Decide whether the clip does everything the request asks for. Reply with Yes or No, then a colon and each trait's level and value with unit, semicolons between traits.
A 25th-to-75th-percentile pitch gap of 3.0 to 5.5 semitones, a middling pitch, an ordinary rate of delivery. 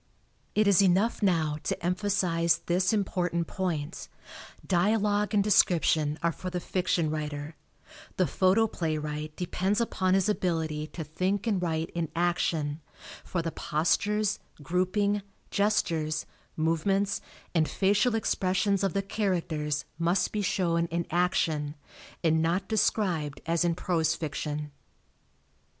No: average, 3.6 semitones; medium, 175 Hz; slow, 125 wpm